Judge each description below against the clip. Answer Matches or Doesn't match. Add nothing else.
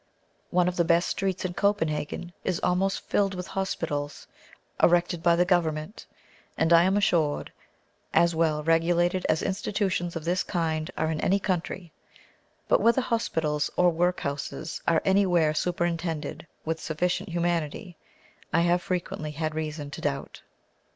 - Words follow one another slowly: Doesn't match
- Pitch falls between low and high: Matches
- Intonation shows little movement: Matches